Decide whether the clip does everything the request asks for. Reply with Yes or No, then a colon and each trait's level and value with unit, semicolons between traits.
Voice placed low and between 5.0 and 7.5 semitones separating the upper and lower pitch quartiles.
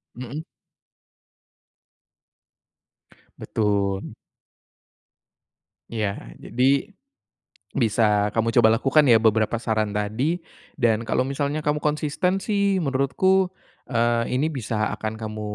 Yes: low, 120 Hz; average, 5.3 semitones